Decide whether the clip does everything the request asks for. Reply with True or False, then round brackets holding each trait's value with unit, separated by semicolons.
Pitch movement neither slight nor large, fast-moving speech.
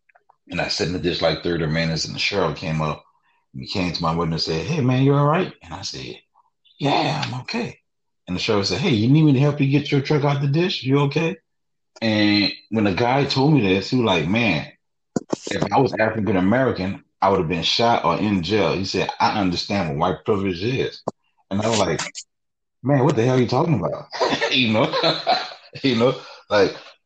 False (7.6 semitones; 225 wpm)